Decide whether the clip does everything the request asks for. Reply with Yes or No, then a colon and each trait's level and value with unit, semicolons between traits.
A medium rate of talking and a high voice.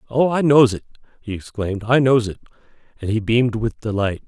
No: average, 195 wpm; low, 115 Hz